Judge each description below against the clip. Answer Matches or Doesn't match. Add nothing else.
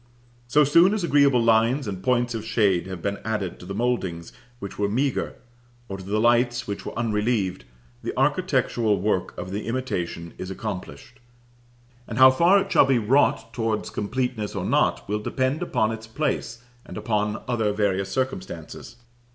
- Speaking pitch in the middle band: Doesn't match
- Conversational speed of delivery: Matches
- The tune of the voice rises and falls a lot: Doesn't match